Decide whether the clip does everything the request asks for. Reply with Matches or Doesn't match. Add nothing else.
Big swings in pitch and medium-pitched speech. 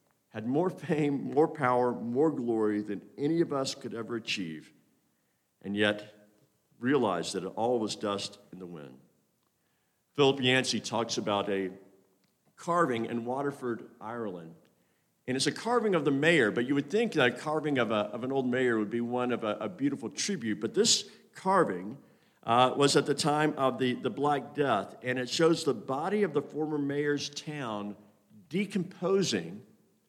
Doesn't match